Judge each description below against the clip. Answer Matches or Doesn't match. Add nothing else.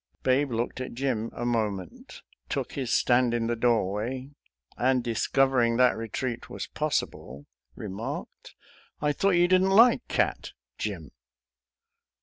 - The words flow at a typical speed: Doesn't match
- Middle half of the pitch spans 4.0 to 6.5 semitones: Doesn't match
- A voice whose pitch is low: Matches